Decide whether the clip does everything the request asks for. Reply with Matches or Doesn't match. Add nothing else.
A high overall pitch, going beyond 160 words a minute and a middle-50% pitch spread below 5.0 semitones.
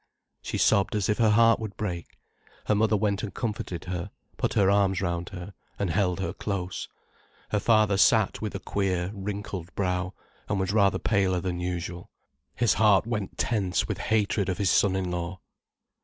Doesn't match